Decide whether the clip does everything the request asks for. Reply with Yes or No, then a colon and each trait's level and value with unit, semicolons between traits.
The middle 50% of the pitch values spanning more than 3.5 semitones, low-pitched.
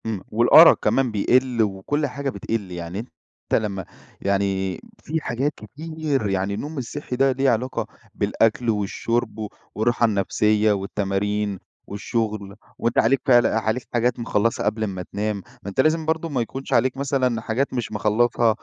Yes: average, 4.1 semitones; low, 115 Hz